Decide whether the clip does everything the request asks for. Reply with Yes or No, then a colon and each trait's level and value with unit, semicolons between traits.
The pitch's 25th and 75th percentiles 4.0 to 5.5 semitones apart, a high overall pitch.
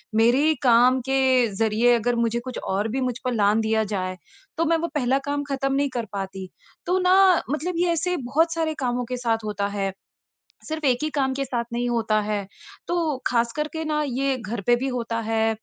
Yes: average, 4.3 semitones; high, 245 Hz